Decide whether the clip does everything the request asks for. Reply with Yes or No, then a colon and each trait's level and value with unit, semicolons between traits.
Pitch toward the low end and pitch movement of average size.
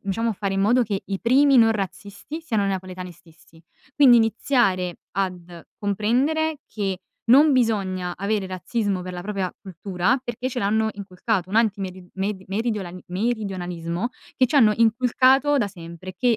No: high, 200 Hz; average, 4.2 semitones